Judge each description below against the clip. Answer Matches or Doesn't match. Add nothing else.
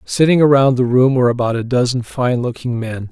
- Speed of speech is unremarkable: Doesn't match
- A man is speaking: Matches